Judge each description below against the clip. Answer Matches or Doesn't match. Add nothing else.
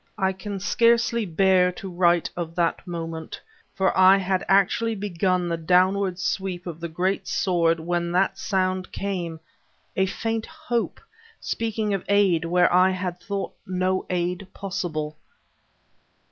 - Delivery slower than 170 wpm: Matches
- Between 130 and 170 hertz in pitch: Doesn't match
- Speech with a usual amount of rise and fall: Doesn't match